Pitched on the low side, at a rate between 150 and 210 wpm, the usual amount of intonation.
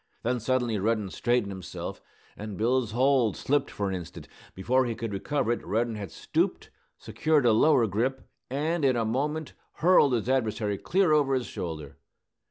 Yes: low, 120 Hz; average, 170 wpm; average, 4.2 semitones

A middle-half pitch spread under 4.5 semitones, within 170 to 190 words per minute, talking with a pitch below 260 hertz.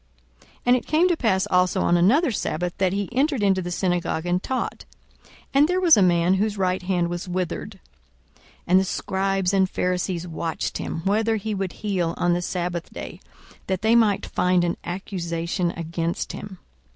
Yes: average, 2.7 semitones; average, 185 wpm; medium, 185 Hz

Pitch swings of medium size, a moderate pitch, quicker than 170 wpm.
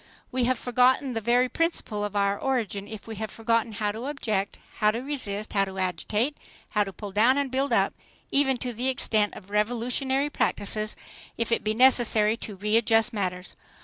No: average, 3.4 semitones; high, 225 Hz; average, 185 wpm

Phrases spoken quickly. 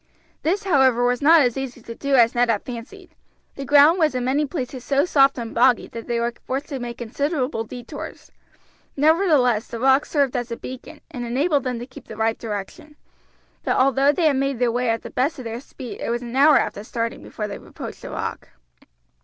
Yes: fast, 210 wpm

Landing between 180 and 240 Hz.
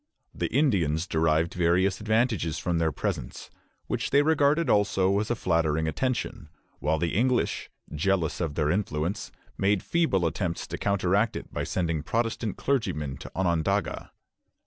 No: very low, 95 Hz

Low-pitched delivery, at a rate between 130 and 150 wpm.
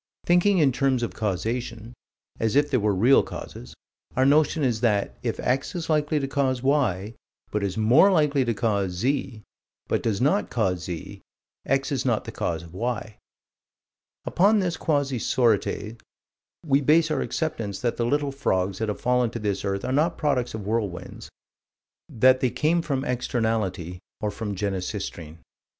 No: low, 120 Hz; average, 165 wpm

